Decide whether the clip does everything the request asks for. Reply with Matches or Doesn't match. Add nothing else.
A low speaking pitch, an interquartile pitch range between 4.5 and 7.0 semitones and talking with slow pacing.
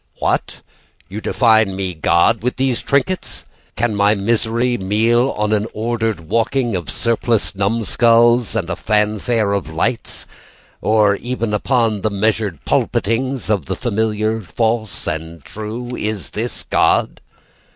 Doesn't match